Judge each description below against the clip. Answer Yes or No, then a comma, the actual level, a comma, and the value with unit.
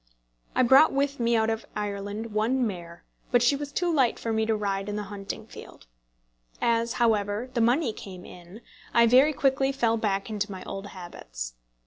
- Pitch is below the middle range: No, high, 225 Hz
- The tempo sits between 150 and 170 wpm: No, average, 185 wpm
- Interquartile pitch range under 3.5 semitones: No, average, 3.8 semitones